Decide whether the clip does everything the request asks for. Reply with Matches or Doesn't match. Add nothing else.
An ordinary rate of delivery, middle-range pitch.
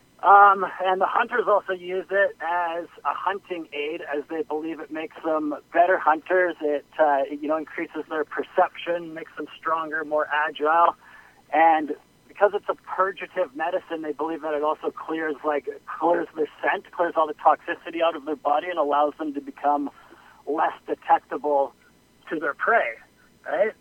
Matches